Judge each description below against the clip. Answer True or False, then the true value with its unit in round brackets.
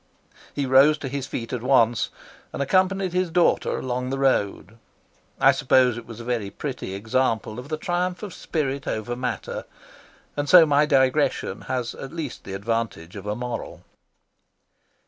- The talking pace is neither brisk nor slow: True (165 wpm)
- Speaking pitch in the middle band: False (130 Hz)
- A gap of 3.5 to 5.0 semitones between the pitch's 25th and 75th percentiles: True (4.2 semitones)